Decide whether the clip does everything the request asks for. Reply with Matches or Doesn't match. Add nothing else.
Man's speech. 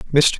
Matches